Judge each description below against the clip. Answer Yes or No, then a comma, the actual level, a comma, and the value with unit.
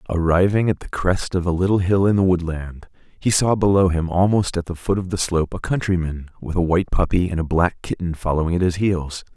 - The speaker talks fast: Yes, fast, 230 wpm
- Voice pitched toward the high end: No, very low, 90 Hz